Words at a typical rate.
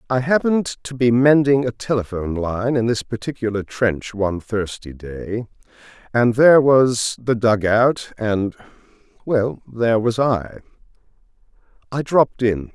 No: slow, 130 wpm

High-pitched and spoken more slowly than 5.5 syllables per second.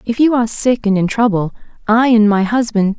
No: high, 220 Hz; 5.6 syllables/s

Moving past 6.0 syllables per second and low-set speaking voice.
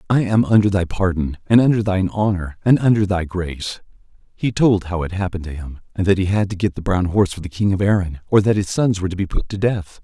Yes: 6.2 syllables/s; very low, 95 Hz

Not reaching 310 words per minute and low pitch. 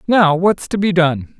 No: fast, 215 wpm; medium, 170 Hz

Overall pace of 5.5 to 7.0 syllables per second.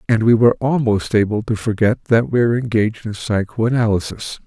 Yes: 5.7 syllables/s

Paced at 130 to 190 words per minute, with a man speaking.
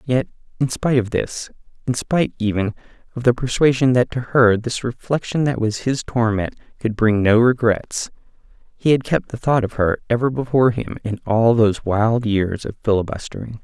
Yes: average, 180 wpm; male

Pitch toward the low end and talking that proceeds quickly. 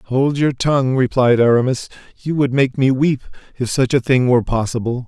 No: low, 130 Hz; average, 190 wpm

